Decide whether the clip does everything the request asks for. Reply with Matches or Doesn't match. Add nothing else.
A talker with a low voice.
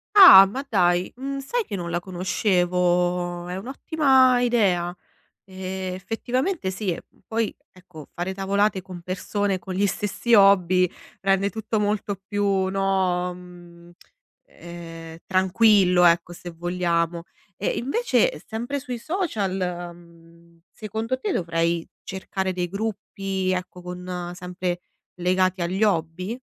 Doesn't match